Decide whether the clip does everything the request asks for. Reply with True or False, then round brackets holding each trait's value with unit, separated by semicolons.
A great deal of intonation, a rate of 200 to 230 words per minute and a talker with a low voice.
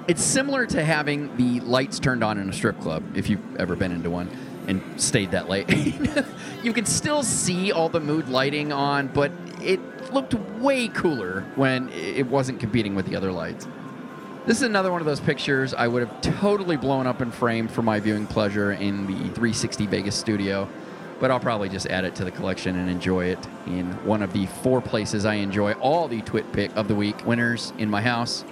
True (7.1 semitones; 205 wpm; 120 Hz)